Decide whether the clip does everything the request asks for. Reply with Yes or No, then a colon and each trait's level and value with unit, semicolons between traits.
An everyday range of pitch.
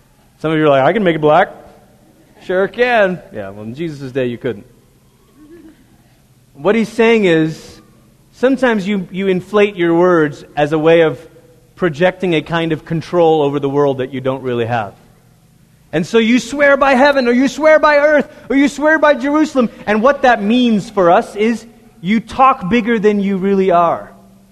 No: wide, 7.5 semitones